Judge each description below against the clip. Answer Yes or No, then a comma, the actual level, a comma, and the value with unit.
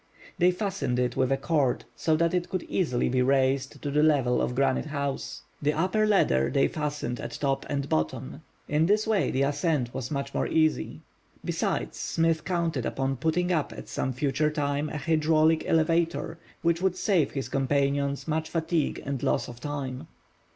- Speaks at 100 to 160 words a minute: No, average, 180 wpm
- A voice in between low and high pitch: Yes, medium, 150 Hz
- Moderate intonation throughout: Yes, average, 3.3 semitones